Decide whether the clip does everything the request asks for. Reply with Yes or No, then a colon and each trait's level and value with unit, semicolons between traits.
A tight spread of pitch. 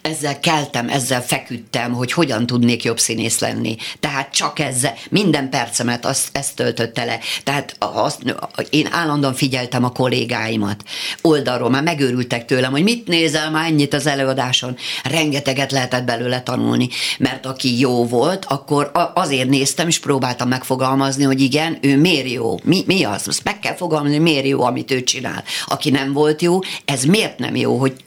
No: average, 3.3 semitones